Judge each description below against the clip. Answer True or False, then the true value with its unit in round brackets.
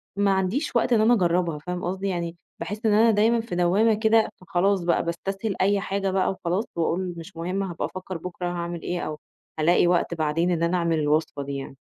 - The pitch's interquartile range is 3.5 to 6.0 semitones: False (2.9 semitones)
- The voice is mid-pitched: True (180 Hz)